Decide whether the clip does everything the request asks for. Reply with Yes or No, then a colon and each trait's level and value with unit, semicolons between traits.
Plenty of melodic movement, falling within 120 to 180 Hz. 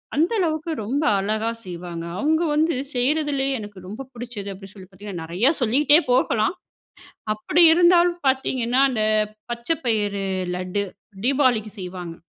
No: wide, 6.4 semitones; high, 235 Hz